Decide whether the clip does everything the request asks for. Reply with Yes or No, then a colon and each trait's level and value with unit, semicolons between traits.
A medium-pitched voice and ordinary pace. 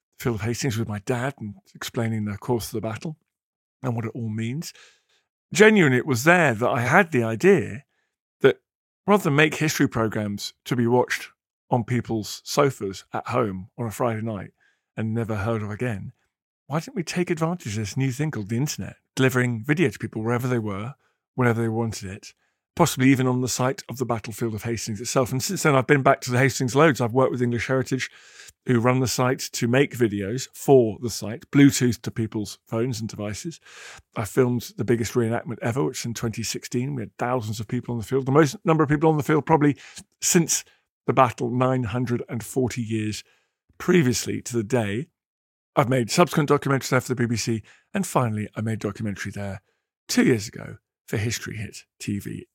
No: low, 125 Hz; average, 195 wpm